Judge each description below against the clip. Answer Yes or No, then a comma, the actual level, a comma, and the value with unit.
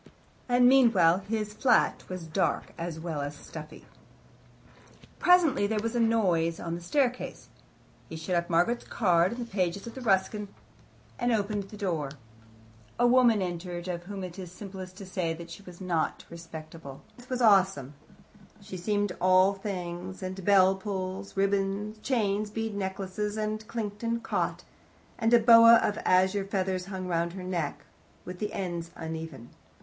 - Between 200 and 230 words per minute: No, average, 160 wpm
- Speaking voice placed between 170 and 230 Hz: Yes, high, 190 Hz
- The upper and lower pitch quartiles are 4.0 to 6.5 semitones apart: No, average, 3.6 semitones